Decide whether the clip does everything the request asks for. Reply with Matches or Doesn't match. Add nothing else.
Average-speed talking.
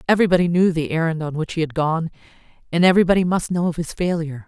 Doesn't match